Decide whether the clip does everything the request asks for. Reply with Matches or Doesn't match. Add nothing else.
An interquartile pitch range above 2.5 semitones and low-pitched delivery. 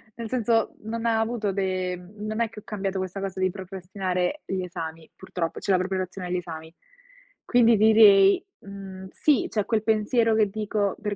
Doesn't match